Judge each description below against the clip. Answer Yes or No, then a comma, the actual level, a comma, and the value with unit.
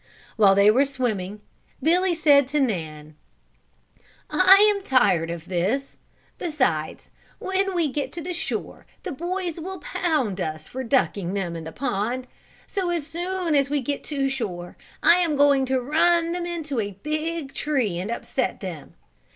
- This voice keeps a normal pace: Yes, average, 160 wpm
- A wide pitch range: Yes, wide, 8.8 semitones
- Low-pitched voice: No, very high, 275 Hz